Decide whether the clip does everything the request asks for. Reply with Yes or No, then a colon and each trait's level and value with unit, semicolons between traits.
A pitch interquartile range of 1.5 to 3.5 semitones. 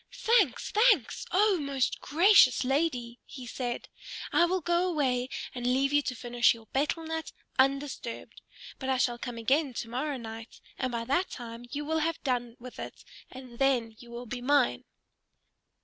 No: average, 4.1 semitones